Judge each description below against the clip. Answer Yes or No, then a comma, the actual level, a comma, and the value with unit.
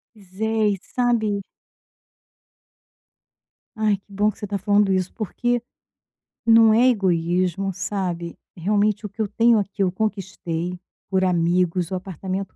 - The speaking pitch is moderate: No, high, 195 Hz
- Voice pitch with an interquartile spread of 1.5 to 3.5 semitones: Yes, average, 2.8 semitones